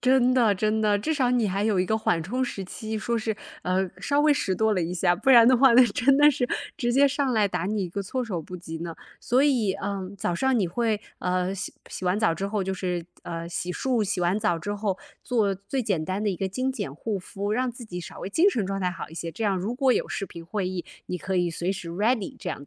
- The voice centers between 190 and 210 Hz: Yes, high, 200 Hz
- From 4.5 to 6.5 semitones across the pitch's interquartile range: Yes, average, 4.8 semitones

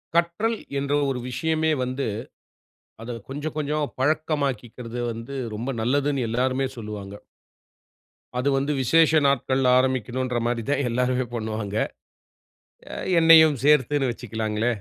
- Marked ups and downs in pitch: No, average, 3.4 semitones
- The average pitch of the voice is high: No, low, 130 Hz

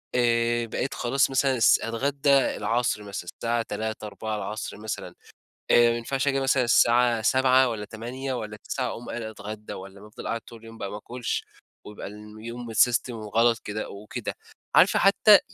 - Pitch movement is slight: Yes, narrow, 2.3 semitones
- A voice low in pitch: Yes, low, 115 Hz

